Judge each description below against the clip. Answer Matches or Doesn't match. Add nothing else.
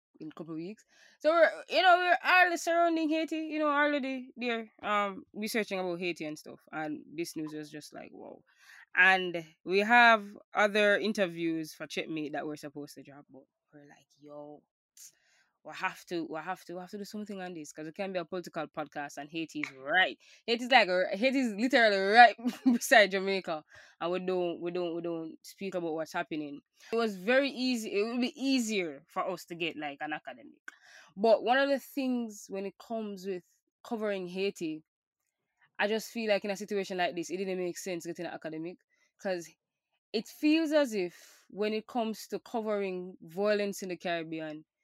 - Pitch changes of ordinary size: Doesn't match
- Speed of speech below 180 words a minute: Doesn't match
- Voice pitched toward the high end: Matches